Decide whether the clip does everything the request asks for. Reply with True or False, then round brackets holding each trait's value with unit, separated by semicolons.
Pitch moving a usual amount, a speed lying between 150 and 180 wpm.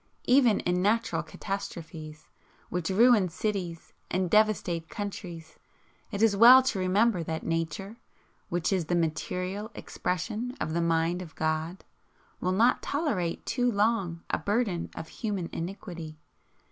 False (4.3 semitones; 135 wpm)